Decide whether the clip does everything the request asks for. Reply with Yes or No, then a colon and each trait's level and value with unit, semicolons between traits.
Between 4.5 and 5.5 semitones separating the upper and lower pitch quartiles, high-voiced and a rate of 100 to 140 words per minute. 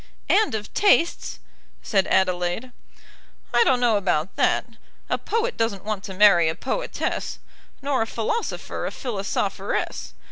Yes: average, 5.2 semitones; high, 215 Hz; slow, 135 wpm